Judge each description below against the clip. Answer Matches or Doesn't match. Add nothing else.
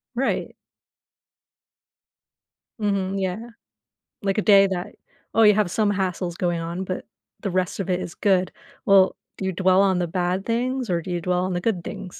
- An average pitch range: Doesn't match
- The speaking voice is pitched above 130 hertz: Matches